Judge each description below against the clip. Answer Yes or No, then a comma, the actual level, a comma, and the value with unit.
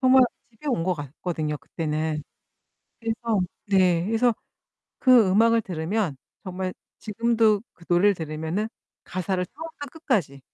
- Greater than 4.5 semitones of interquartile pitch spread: Yes, wide, 5.4 semitones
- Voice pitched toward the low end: No, high, 195 Hz